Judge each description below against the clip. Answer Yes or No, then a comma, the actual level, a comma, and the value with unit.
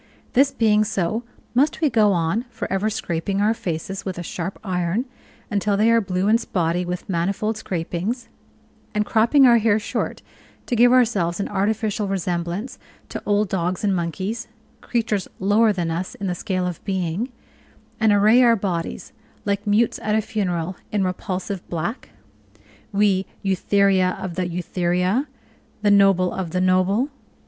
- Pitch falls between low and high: No, high, 195 Hz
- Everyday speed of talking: Yes, average, 155 wpm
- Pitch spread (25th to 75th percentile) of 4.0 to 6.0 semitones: No, average, 3.2 semitones